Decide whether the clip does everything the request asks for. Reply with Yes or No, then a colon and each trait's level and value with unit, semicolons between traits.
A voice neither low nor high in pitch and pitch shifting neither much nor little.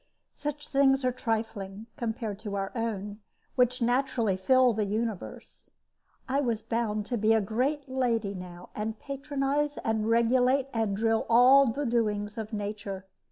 No: high, 230 Hz; average, 3.5 semitones